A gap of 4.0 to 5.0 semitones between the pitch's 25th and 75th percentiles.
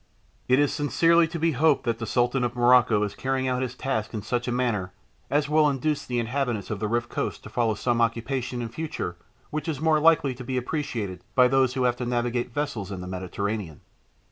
No: average, 3.4 semitones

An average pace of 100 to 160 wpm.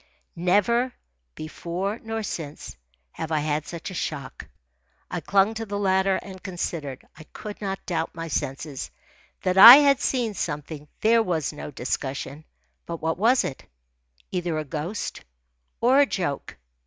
Yes: average, 150 wpm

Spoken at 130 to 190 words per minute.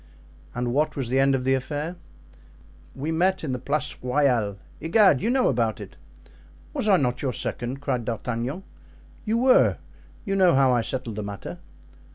Yes: average, 170 wpm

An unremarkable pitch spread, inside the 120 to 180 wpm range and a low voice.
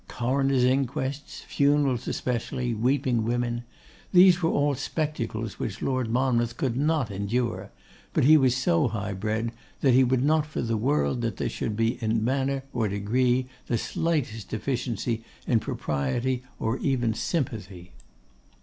Yes: average, 3.3 semitones; average, 145 wpm; low, 125 Hz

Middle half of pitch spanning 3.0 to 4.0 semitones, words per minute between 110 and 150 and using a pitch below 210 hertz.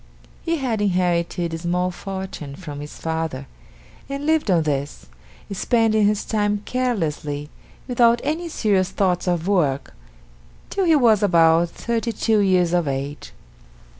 No: wide, 5.6 semitones; slow, 135 wpm; medium, 185 Hz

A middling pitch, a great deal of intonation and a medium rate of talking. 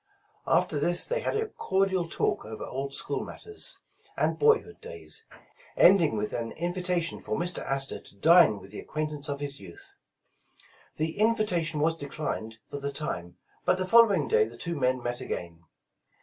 Yes: medium, 155 Hz; wide, 6.4 semitones; average, 165 wpm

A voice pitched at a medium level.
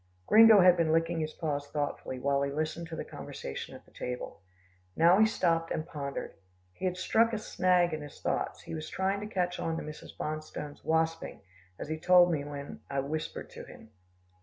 Yes: medium, 160 Hz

